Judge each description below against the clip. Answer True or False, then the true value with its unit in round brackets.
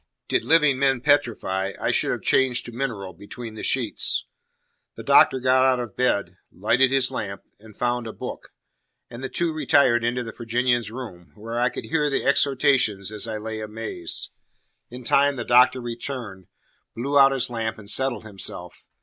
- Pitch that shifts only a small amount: False (3.4 semitones)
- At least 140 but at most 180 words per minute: True (175 wpm)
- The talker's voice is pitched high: False (120 Hz)